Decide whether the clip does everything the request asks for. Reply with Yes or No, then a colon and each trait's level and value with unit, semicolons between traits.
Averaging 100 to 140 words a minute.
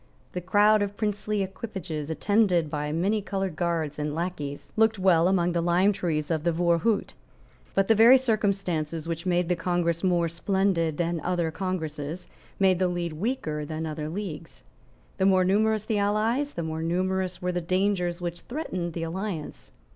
No: average, 165 wpm